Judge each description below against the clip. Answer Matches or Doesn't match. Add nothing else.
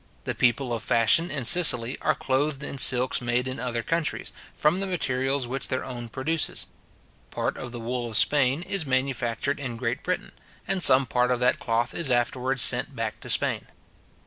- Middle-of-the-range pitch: Doesn't match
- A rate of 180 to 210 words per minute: Matches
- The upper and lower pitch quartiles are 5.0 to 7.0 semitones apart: Doesn't match